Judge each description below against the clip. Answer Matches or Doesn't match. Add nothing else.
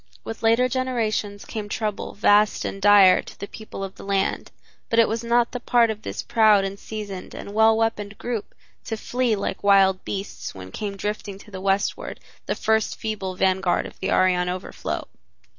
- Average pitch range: Doesn't match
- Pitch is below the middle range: Doesn't match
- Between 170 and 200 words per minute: Matches